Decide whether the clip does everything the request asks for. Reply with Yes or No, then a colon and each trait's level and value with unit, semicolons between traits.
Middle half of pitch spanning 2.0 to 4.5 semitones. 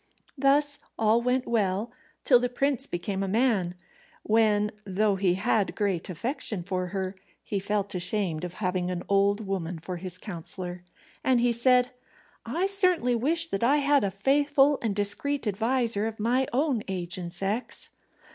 No: average, 5.0 semitones